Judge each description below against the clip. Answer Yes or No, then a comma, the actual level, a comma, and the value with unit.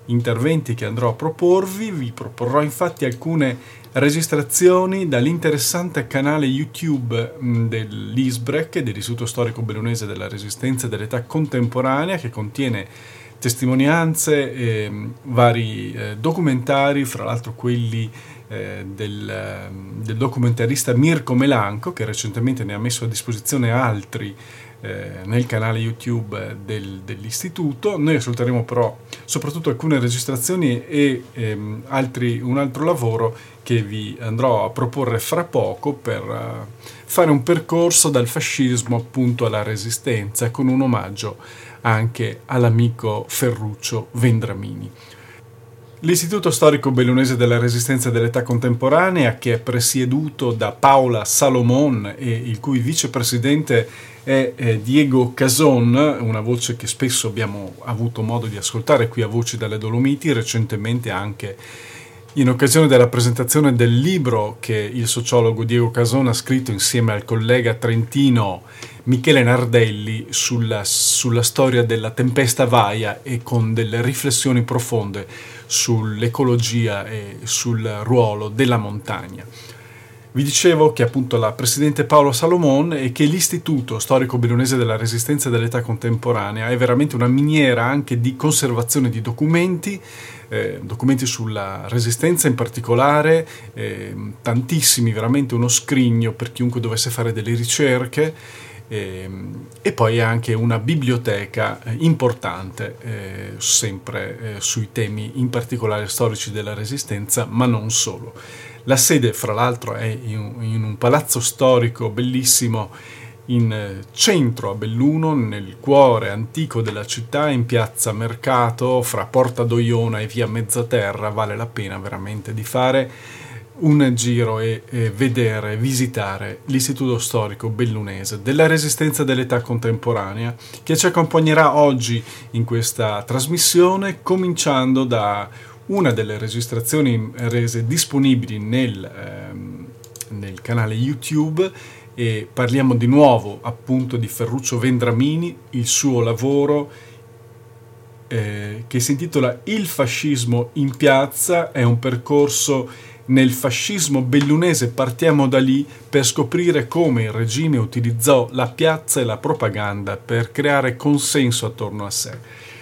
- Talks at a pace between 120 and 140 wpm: Yes, average, 125 wpm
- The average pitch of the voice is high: No, low, 120 Hz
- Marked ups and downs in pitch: No, average, 2.8 semitones